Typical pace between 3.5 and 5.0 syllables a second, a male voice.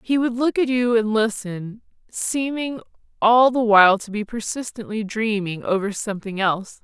No: 4.8 syllables/s; female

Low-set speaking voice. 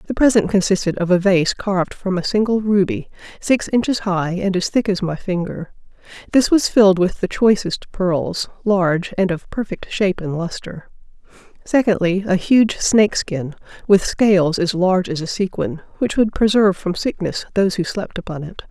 No: high, 190 Hz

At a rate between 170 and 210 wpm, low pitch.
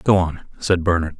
Yes: average, 200 wpm; very low, 85 Hz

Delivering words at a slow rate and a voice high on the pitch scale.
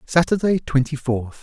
No: slow, 125 wpm; medium, 145 Hz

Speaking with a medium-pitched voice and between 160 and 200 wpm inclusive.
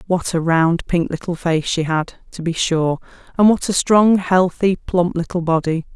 Yes: medium, 175 Hz; average, 190 wpm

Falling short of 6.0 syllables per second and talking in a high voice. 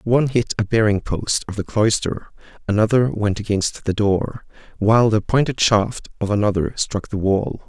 No: 4.8 syllables/s; low, 105 Hz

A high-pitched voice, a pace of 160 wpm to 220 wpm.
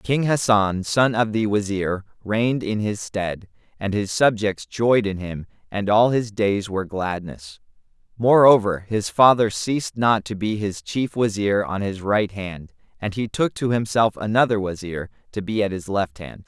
No: low, 105 Hz; average, 180 wpm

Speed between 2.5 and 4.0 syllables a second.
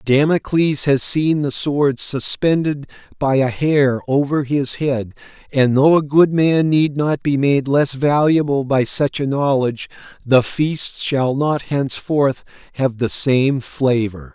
Yes: 3.8 syllables/s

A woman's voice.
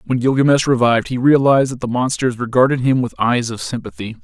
No: male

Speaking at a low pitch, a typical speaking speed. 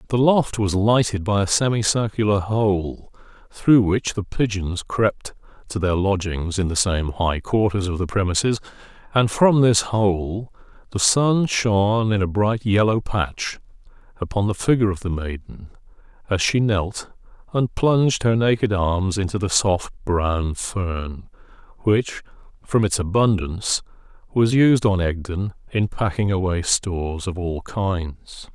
Yes: low, 100 Hz; average, 145 wpm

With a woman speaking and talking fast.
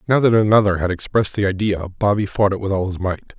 No: male; fast, 250 wpm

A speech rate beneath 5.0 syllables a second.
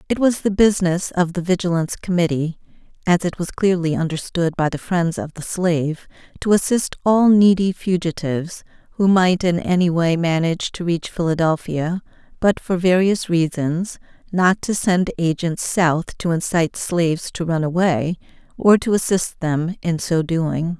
Yes: 4.7 syllables/s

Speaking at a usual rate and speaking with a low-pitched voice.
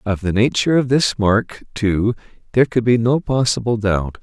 Yes: average, 185 wpm; low, 115 Hz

